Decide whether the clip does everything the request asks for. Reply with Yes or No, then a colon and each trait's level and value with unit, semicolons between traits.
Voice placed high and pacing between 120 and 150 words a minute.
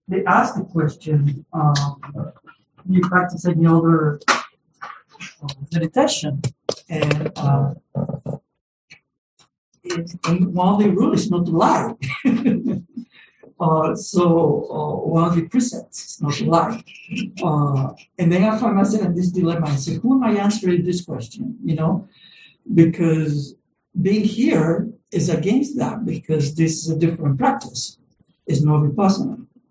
No: medium, 170 Hz; average, 140 wpm